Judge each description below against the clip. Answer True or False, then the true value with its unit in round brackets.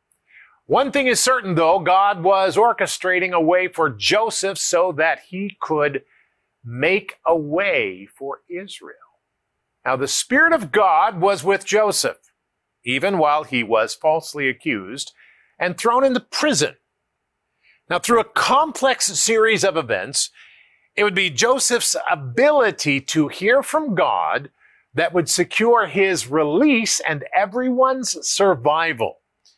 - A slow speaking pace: True (130 wpm)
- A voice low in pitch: False (195 Hz)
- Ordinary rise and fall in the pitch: False (6.9 semitones)